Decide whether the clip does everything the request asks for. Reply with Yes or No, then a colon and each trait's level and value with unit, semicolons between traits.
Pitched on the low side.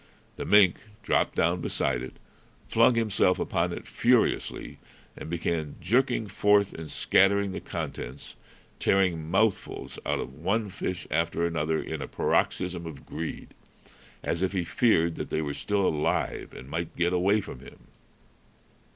Yes: very low, 90 Hz